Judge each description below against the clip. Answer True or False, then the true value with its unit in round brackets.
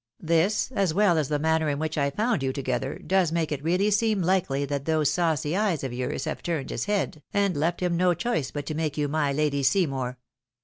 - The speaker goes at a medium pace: False (225 wpm)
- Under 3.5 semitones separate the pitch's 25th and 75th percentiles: False (4.4 semitones)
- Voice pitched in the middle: True (160 Hz)